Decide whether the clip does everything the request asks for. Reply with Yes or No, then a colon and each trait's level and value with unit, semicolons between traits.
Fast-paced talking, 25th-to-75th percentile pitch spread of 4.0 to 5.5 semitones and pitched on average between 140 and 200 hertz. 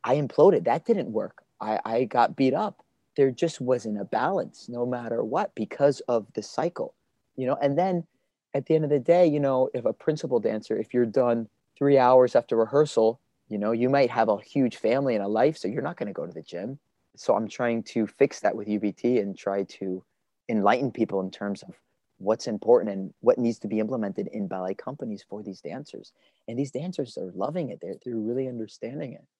No: fast, 215 wpm; average, 4.7 semitones; low, 120 Hz